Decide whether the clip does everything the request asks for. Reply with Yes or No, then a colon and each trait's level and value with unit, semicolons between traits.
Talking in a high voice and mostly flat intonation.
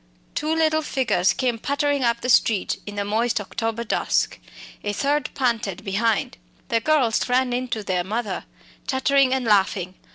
No: high, 235 Hz; average, 4.3 semitones